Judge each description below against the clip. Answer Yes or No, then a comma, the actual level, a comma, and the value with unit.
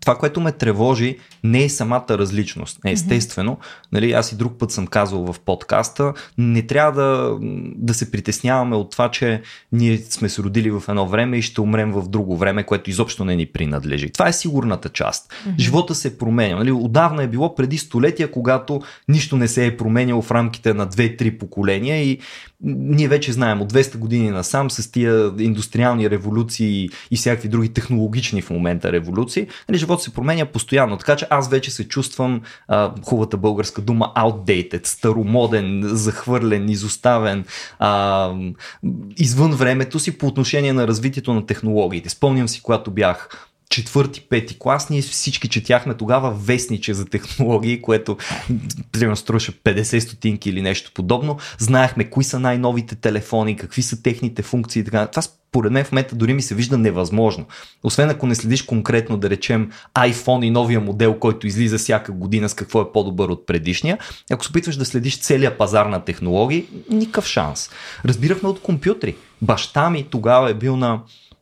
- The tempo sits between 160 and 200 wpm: Yes, fast, 165 wpm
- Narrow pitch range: No, average, 3.7 semitones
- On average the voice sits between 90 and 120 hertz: Yes, low, 115 Hz